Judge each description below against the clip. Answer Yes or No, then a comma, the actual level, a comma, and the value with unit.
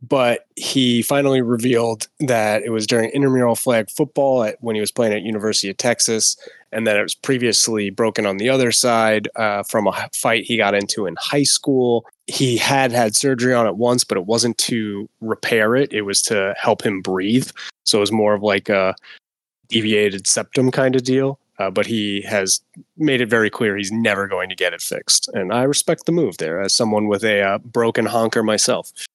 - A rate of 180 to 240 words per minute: Yes, fast, 205 wpm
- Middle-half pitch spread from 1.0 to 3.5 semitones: Yes, average, 3.1 semitones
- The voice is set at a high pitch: No, low, 115 Hz